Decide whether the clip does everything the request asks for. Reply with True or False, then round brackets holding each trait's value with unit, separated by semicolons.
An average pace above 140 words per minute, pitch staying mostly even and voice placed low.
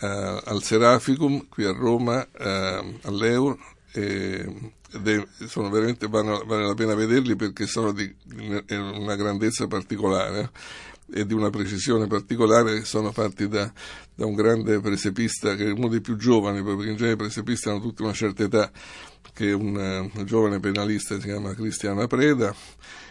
True (165 wpm; 1.9 semitones; 105 Hz)